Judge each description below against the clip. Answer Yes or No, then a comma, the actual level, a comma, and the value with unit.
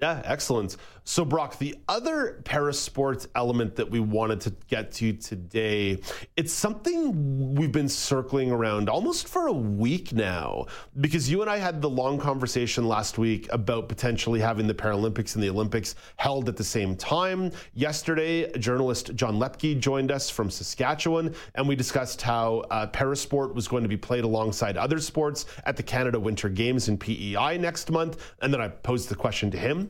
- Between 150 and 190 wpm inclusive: Yes, average, 175 wpm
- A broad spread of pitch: No, average, 4.9 semitones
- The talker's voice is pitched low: Yes, low, 125 Hz